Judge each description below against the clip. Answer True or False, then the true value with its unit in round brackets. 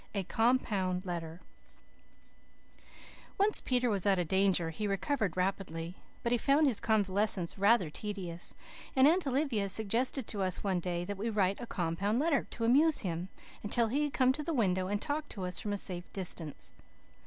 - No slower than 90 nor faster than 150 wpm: False (175 wpm)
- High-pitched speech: True (200 Hz)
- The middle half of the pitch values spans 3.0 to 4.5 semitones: False (5.1 semitones)